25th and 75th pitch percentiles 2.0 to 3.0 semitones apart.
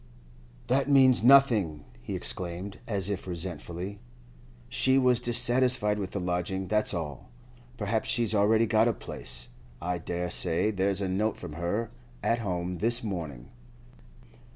No: average, 4.7 semitones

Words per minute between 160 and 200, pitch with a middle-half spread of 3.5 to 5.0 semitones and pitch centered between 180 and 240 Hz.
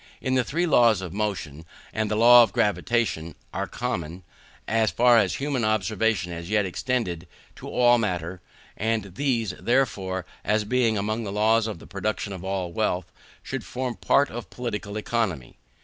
No: average, 165 wpm; average, 4.0 semitones; low, 110 Hz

